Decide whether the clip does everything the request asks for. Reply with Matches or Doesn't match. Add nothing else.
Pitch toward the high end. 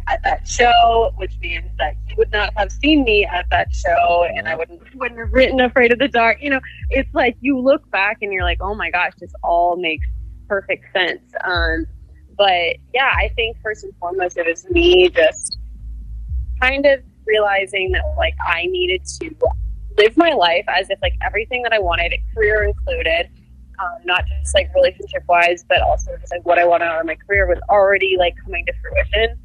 Matches